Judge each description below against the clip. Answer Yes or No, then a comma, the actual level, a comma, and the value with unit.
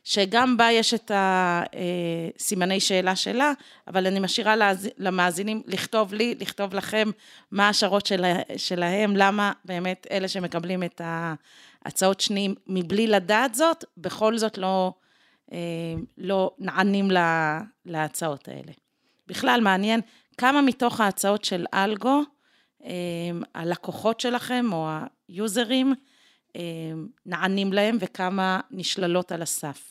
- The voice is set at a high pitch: Yes, high, 195 Hz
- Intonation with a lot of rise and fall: No, average, 3.6 semitones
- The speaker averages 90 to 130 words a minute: Yes, average, 110 wpm